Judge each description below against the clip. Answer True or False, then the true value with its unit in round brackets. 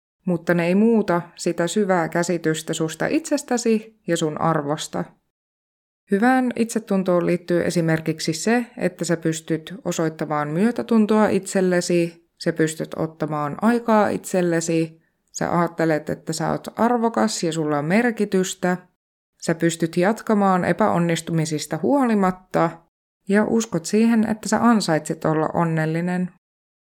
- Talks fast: False (115 wpm)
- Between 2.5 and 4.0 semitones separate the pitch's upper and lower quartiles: False (4.5 semitones)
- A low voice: False (175 Hz)